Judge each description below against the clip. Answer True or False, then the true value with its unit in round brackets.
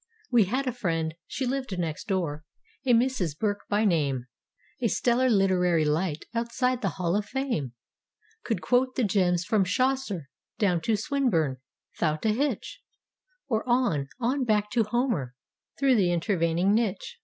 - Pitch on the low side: False (205 Hz)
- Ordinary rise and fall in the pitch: False (6.6 semitones)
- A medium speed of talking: True (150 wpm)